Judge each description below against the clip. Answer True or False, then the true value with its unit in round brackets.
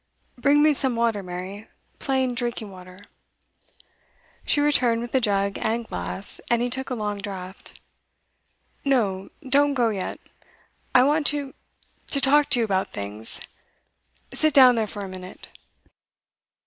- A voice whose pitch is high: True (230 Hz)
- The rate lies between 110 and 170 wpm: True (145 wpm)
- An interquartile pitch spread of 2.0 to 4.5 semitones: False (5.4 semitones)